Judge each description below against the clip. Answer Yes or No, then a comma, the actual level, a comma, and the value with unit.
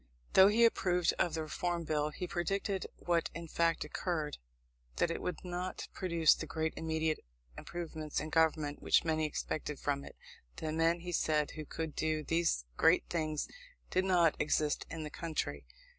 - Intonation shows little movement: Yes, narrow, 2.1 semitones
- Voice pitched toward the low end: No, medium, 160 Hz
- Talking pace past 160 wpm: Yes, average, 170 wpm